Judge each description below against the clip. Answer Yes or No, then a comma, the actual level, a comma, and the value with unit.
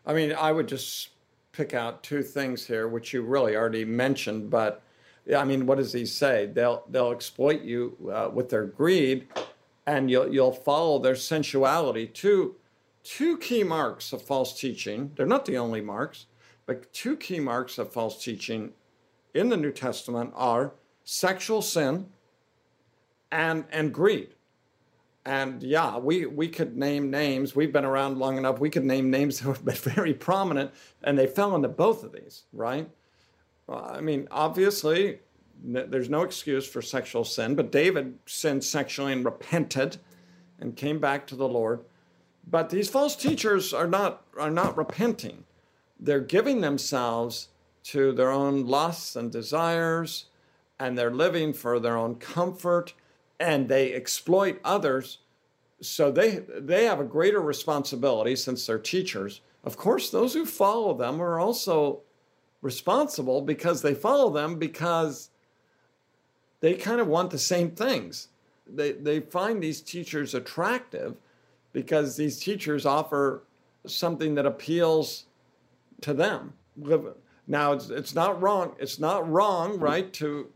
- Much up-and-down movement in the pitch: No, average, 4.3 semitones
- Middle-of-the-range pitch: Yes, medium, 145 Hz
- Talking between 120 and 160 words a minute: Yes, average, 150 wpm